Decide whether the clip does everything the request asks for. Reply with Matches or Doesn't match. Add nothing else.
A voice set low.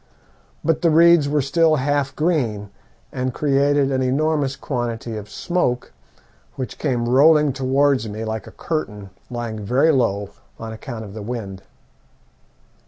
Matches